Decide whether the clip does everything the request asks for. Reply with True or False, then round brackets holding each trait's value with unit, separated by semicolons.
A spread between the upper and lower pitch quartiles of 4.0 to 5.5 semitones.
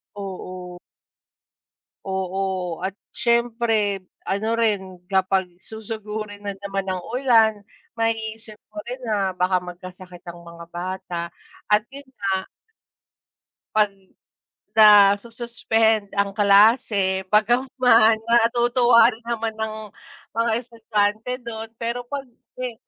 False (3.2 semitones)